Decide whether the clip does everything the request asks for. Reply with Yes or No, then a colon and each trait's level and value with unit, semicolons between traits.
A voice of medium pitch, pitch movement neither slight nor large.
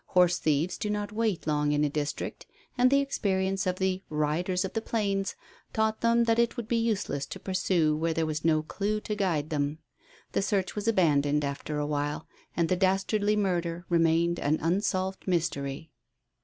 Yes: medium, 180 Hz; average, 5.0 semitones